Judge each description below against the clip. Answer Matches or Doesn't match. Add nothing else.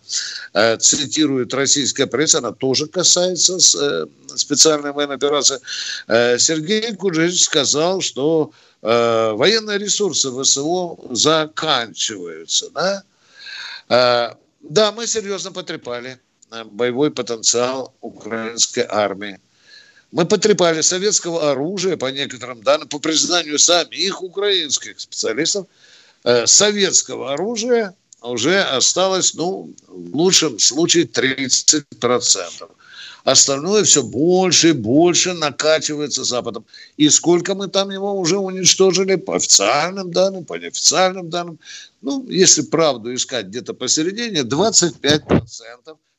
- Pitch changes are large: Matches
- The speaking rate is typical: Doesn't match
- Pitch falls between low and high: Matches